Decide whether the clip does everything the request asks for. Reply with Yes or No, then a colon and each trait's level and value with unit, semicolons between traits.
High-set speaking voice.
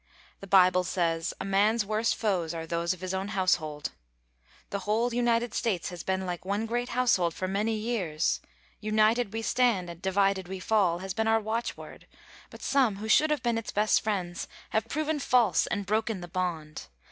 Yes: high, 200 Hz